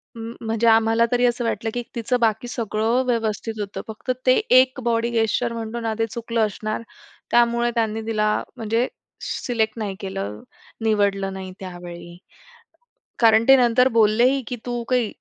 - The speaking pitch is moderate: No, high, 225 Hz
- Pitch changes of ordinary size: No, narrow, 1.9 semitones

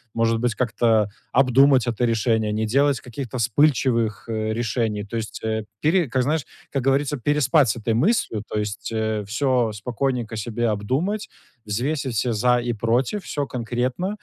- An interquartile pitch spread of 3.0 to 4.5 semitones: Yes, average, 3.6 semitones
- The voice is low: Yes, low, 120 Hz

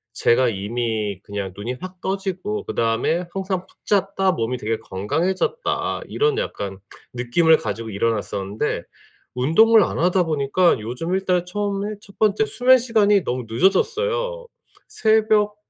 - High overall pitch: No, medium, 180 Hz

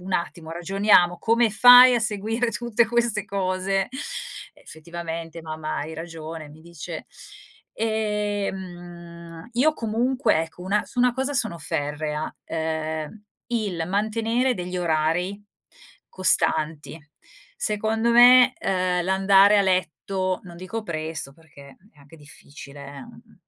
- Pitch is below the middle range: No, medium, 185 Hz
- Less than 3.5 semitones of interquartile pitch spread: No, average, 5.1 semitones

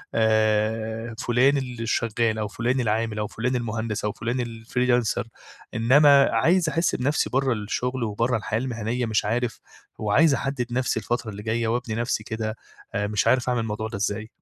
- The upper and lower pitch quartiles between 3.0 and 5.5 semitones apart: No, narrow, 2.4 semitones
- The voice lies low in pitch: Yes, low, 115 Hz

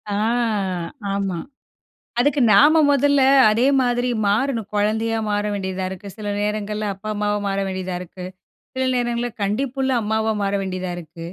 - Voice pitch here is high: Yes, high, 210 Hz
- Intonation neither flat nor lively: Yes, average, 3.8 semitones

